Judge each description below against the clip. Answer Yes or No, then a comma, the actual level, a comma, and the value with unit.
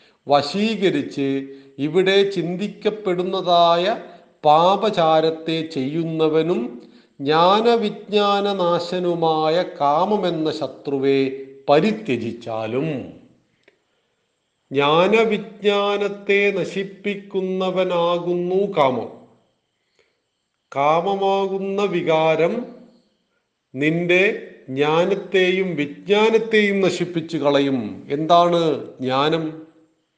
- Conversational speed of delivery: No, slow, 45 wpm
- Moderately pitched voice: Yes, medium, 175 Hz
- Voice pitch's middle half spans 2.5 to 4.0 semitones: No, average, 4.6 semitones